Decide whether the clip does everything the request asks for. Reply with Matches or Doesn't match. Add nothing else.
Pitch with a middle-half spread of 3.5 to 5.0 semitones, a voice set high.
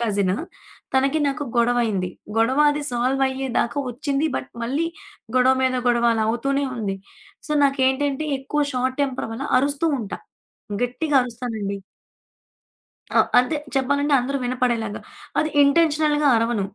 Doesn't match